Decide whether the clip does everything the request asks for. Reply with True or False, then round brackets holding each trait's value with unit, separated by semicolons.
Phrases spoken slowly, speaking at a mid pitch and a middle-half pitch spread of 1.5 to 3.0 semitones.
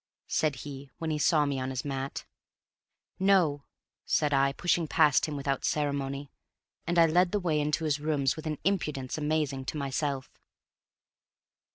False (160 wpm; 150 Hz; 2.4 semitones)